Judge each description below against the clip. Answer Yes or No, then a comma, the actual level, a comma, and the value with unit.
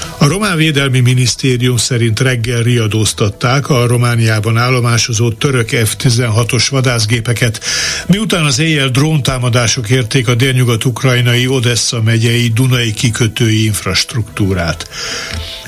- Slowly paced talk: Yes, slow, 95 wpm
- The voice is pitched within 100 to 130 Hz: Yes, low, 120 Hz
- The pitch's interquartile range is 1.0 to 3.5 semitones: Yes, narrow, 2.4 semitones